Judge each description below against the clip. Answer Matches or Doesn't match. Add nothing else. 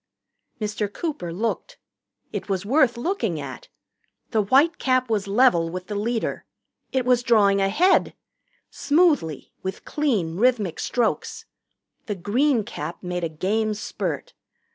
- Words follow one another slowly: Matches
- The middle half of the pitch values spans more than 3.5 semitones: Matches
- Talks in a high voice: Matches